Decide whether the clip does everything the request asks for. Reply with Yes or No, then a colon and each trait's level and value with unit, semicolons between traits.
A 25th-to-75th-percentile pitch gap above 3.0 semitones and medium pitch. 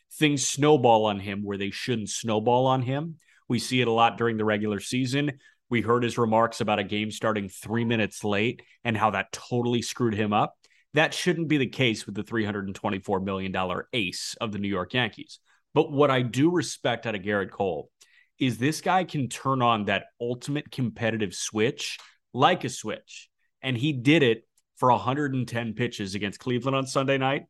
No: average, 4.0 semitones; low, 120 Hz